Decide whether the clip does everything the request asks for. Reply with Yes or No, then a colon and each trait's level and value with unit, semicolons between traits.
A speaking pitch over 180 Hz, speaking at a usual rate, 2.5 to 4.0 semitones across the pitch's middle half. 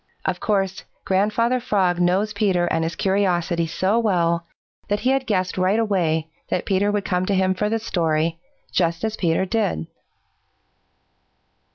Yes: high, 190 Hz; average, 155 wpm; average, 3.4 semitones